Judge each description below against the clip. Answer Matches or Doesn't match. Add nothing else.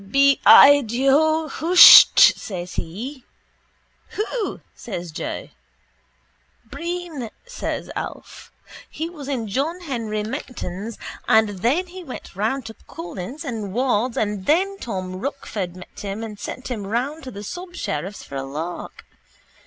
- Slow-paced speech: Matches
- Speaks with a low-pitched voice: Doesn't match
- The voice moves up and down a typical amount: Doesn't match